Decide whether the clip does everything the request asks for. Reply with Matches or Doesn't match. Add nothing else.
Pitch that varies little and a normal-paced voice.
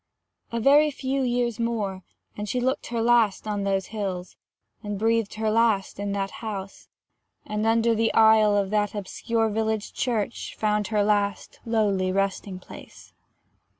Matches